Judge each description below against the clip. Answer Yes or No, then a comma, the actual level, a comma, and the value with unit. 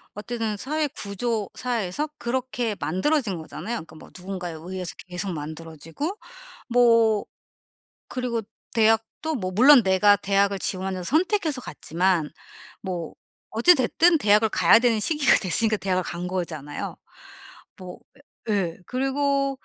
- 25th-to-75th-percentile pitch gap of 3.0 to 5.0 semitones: No, wide, 5.5 semitones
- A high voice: Yes, high, 210 Hz